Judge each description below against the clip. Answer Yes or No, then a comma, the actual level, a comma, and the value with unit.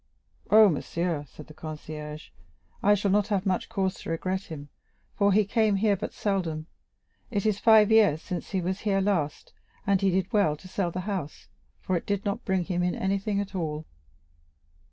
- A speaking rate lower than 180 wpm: No, average, 190 wpm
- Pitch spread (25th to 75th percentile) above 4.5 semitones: No, average, 3.6 semitones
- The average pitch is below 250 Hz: Yes, high, 190 Hz